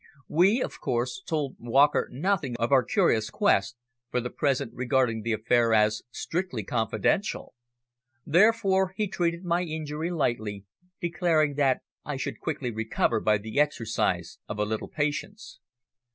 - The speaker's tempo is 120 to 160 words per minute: Yes, average, 140 wpm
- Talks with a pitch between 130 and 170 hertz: Yes, low, 135 Hz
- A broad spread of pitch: Yes, wide, 7.0 semitones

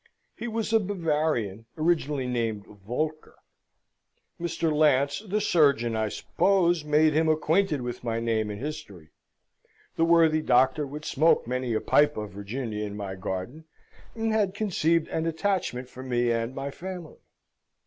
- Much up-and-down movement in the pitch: Yes, wide, 6.1 semitones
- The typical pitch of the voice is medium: Yes, medium, 150 Hz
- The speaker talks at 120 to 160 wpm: Yes, average, 150 wpm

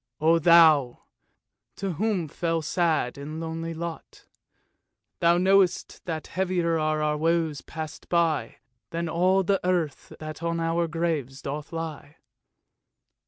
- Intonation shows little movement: Yes, narrow, 1.8 semitones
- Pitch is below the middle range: No, medium, 165 Hz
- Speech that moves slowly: Yes, slow, 125 wpm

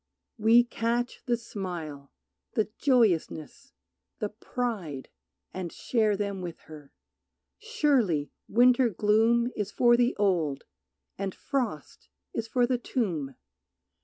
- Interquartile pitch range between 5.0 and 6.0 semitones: Yes, wide, 5.5 semitones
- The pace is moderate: No, slow, 110 wpm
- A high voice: Yes, high, 215 Hz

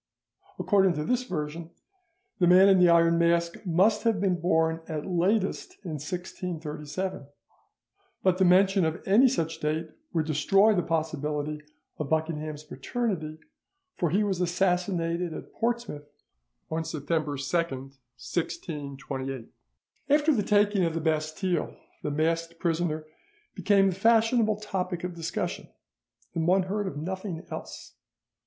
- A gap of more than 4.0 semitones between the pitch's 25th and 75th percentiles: No, average, 3.6 semitones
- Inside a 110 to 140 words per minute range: Yes, slow, 135 wpm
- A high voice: No, medium, 170 Hz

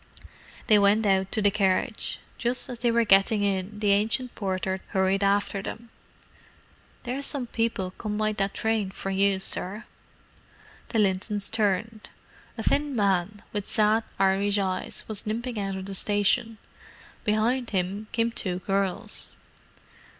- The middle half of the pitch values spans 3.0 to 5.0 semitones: No, narrow, 2.5 semitones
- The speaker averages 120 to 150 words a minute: Yes, average, 145 wpm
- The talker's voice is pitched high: Yes, high, 205 Hz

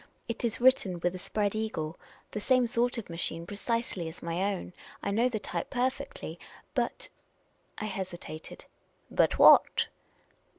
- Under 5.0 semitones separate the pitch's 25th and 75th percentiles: No, wide, 5.4 semitones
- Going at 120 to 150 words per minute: No, average, 160 wpm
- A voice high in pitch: Yes, high, 210 Hz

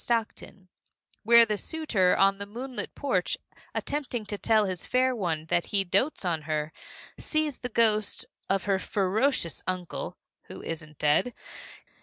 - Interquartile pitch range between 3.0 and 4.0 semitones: No, average, 4.9 semitones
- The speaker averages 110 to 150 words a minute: Yes, average, 145 wpm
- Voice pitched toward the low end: No, high, 205 Hz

